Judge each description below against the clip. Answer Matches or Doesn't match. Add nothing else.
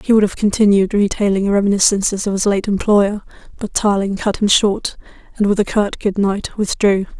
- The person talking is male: Doesn't match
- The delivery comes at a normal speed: Matches